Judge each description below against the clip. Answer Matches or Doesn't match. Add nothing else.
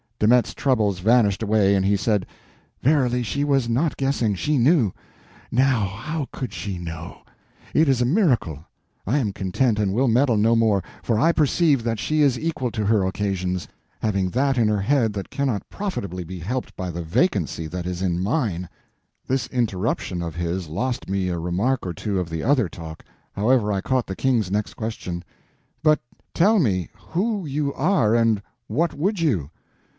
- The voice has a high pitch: Doesn't match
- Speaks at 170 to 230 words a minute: Matches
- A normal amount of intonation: Doesn't match